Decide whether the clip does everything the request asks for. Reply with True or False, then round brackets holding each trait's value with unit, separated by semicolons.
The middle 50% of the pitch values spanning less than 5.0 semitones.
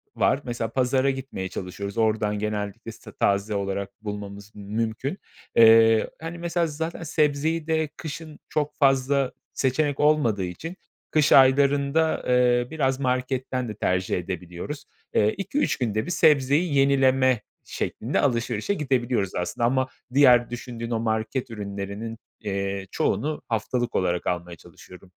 False (5.3 semitones)